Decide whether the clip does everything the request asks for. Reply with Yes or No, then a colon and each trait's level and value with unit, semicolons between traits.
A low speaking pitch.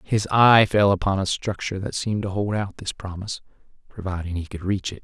Yes: very low, 95 Hz